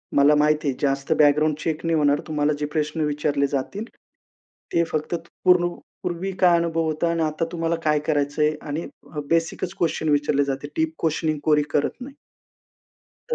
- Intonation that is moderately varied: No, narrow, 2.2 semitones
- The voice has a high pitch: No, medium, 155 Hz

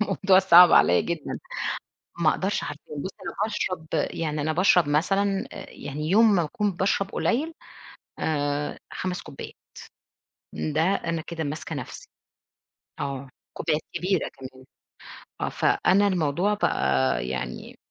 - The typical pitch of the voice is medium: Yes, medium, 170 Hz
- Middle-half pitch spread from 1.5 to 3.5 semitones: No, average, 4.8 semitones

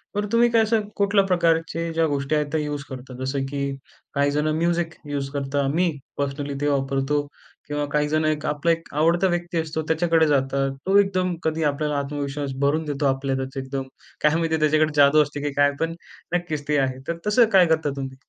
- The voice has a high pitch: No, medium, 150 Hz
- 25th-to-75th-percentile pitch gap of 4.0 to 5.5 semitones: No, average, 2.8 semitones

